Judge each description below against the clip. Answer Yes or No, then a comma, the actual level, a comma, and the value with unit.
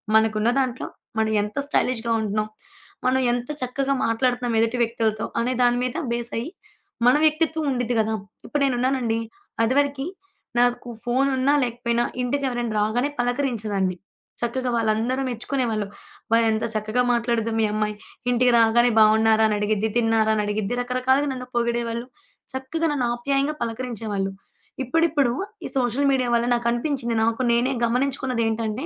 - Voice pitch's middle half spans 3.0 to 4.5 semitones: No, narrow, 2.5 semitones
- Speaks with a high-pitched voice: Yes, high, 240 Hz